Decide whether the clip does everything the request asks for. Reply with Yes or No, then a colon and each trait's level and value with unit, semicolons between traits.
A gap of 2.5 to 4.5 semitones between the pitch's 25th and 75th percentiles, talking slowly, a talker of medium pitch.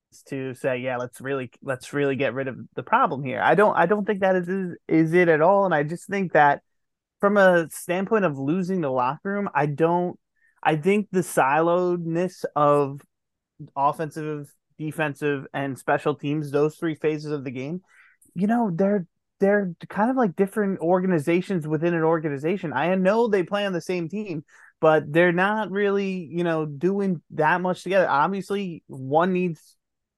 No: average, 4.2 semitones; average, 175 wpm; medium, 170 Hz